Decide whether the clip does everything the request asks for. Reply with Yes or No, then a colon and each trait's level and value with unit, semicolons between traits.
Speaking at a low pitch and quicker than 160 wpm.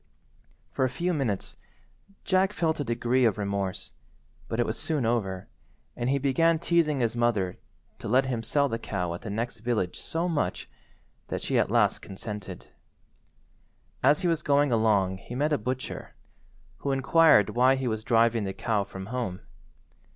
Yes: low, 120 Hz; average, 170 wpm